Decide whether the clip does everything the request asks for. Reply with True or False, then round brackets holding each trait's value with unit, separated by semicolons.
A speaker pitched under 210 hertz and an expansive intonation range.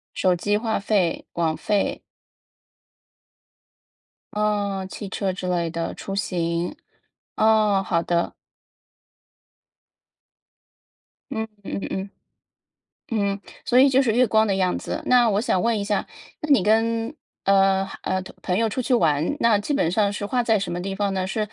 False (200 Hz; 2.9 semitones)